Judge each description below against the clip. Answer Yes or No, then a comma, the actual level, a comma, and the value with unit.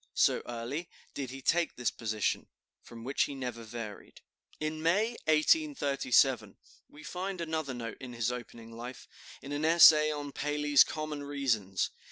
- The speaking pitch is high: No, medium, 140 Hz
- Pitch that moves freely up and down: No, average, 4.4 semitones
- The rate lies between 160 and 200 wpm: No, average, 150 wpm